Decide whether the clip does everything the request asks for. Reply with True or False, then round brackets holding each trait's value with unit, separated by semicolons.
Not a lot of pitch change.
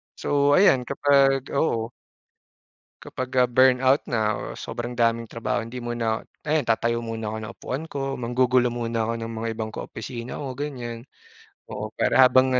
True (2.3 semitones)